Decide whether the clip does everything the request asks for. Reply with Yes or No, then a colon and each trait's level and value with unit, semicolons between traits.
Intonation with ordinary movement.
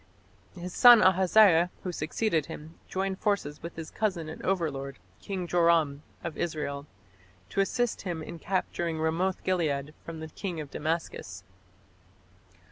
Yes: average, 3.2 semitones